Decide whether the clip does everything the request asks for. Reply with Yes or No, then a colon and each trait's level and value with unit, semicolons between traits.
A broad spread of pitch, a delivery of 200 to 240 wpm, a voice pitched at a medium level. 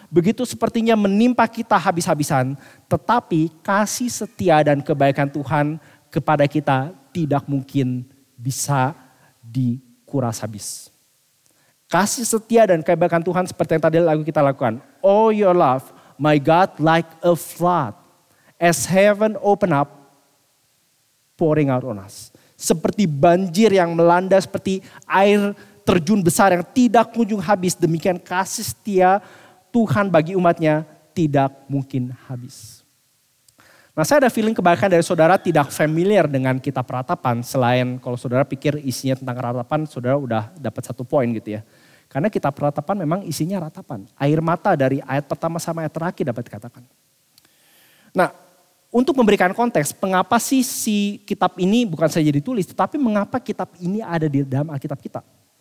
No: wide, 5.9 semitones; average, 140 wpm; medium, 160 Hz